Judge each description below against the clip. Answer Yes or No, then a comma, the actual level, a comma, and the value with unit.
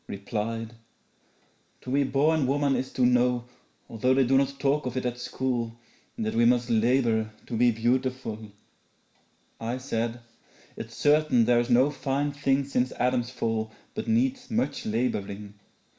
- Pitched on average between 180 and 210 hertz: No, low, 125 Hz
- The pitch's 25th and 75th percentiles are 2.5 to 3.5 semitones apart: Yes, average, 2.9 semitones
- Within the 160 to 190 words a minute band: No, average, 150 wpm